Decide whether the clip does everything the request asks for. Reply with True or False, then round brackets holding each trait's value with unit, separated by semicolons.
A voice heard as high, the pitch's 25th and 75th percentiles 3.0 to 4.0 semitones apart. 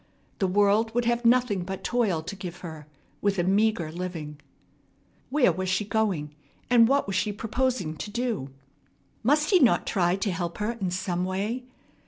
False (200 Hz; 4.5 semitones)